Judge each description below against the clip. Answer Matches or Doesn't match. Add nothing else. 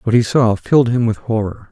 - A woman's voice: Doesn't match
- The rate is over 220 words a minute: Matches